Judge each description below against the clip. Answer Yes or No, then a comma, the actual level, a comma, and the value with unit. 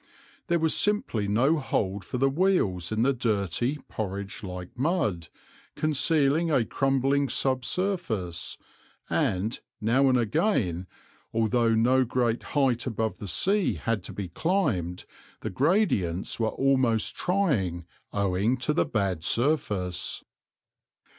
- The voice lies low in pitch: Yes, low, 120 Hz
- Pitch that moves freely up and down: Yes, wide, 6.3 semitones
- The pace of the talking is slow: Yes, slow, 125 wpm